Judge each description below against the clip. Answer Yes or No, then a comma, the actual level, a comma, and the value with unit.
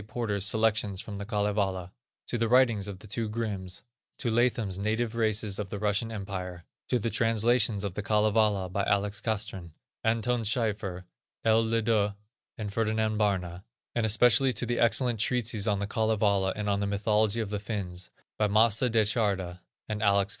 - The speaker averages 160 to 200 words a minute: Yes, average, 170 wpm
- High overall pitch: No, low, 105 Hz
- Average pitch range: No, narrow, 2.2 semitones